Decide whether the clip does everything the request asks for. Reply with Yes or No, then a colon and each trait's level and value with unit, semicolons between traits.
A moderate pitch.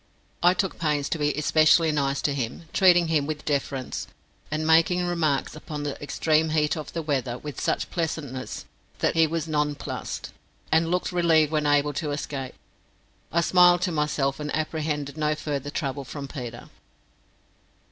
Yes: medium, 150 Hz